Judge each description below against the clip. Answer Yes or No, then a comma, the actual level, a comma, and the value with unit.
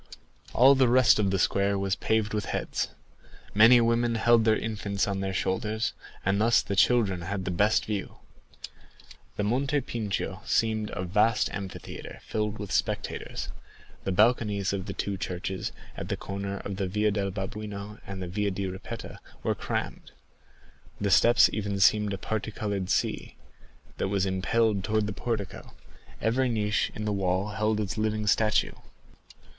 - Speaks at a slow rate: No, average, 160 wpm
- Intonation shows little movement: Yes, narrow, 2.1 semitones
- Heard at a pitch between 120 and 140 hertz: No, low, 105 Hz